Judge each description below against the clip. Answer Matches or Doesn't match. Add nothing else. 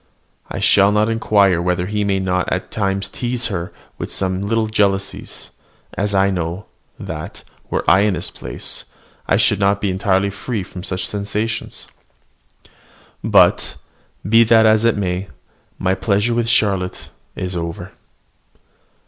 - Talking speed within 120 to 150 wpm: Matches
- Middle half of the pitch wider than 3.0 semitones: Doesn't match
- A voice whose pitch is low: Matches